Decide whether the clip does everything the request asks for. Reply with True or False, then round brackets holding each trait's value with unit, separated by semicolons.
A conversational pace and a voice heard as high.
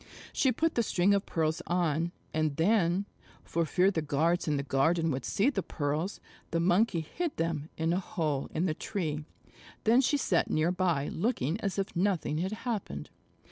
False (180 wpm; 170 Hz)